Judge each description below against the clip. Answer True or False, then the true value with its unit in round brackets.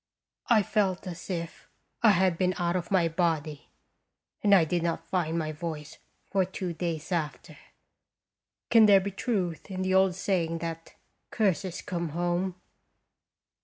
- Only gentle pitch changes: True (2.3 semitones)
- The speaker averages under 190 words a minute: True (150 wpm)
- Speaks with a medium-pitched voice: True (175 Hz)